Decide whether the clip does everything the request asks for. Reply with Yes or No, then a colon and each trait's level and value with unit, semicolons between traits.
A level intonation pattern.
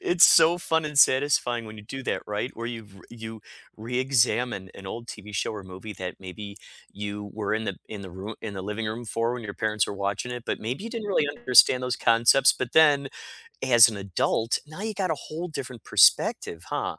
No: average, 4.2 semitones